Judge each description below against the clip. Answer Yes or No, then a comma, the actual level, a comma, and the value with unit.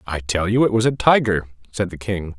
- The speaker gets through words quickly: Yes, fast, 250 wpm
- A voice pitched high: No, low, 100 Hz